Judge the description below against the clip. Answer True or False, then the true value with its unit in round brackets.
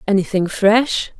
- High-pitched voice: True (205 Hz)